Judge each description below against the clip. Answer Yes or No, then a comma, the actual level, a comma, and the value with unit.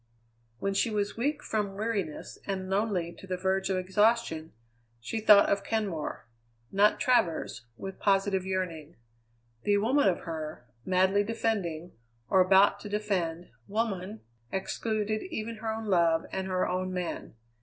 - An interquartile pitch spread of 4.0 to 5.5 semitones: No, average, 2.8 semitones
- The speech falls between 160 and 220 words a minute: No, average, 145 wpm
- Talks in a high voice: Yes, high, 195 Hz